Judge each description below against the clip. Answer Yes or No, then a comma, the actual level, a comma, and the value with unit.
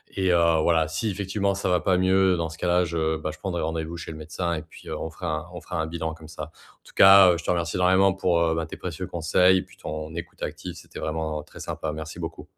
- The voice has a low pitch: Yes, very low, 85 Hz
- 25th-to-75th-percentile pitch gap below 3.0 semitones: Yes, narrow, 2.4 semitones